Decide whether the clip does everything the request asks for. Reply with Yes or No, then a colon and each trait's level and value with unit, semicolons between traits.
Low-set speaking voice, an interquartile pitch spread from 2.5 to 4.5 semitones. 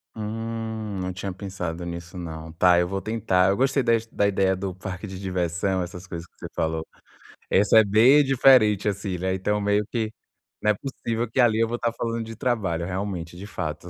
Yes: low, 100 Hz; average, 3.7 semitones